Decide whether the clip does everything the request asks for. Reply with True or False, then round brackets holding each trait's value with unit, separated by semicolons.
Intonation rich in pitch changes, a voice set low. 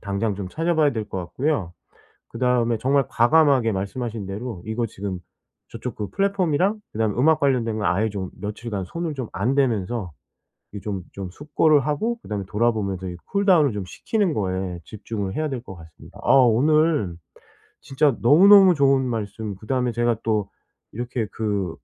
True (5.9 semitones; 115 Hz)